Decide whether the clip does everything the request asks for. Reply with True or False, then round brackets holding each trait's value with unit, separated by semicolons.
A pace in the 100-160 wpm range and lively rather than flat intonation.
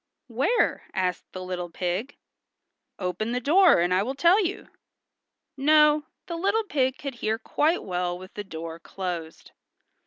True (150 wpm; 8.8 semitones)